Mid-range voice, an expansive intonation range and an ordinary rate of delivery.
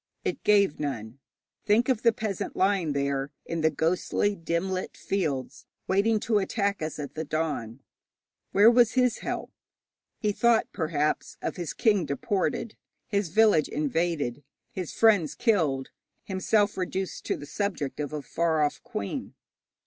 Yes: medium, 175 Hz; wide, 5.7 semitones; average, 150 wpm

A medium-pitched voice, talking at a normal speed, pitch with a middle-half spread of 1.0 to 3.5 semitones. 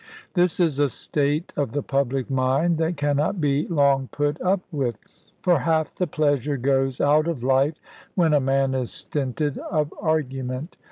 Yes: medium, 145 Hz; average, 165 wpm; average, 2.8 semitones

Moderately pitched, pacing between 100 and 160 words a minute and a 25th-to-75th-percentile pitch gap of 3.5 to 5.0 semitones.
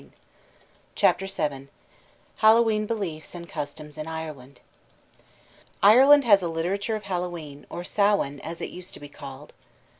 No: medium, 175 Hz; average, 140 wpm; wide, 5.4 semitones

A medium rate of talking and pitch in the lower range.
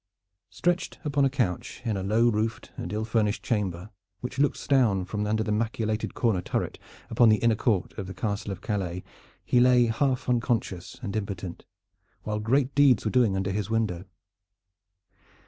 Yes: average, 170 wpm; low, 110 Hz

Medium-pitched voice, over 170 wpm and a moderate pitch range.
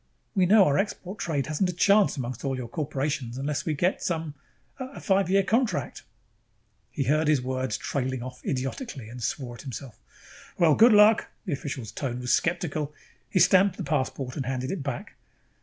No: medium, 150 Hz; average, 180 wpm; wide, 6.1 semitones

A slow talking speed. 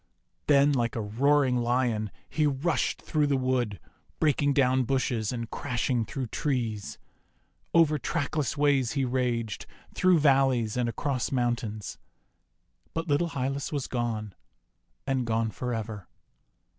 Yes: slow, 130 wpm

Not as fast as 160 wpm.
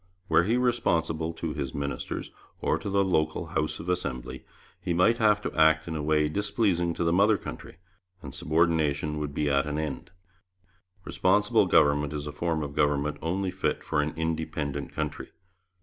No: average, 175 wpm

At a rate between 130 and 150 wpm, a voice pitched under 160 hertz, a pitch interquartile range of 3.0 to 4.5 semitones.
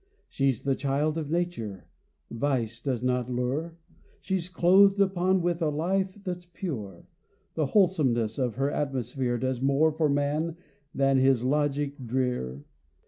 No: average, 140 wpm; medium, 140 Hz; average, 5.1 semitones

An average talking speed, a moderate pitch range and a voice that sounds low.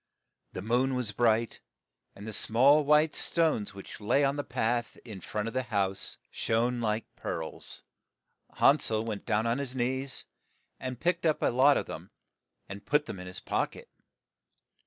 Yes: average, 175 wpm; average, 4.2 semitones; low, 120 Hz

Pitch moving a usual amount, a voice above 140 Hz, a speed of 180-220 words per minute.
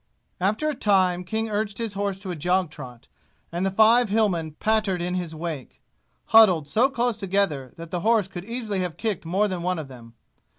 Yes: average, 4.2 semitones; high, 190 Hz; average, 200 wpm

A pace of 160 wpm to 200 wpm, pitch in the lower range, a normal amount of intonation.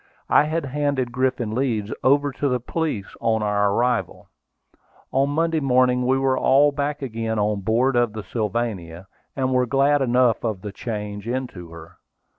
Yes: average, 165 wpm; low, 125 Hz; average, 4.1 semitones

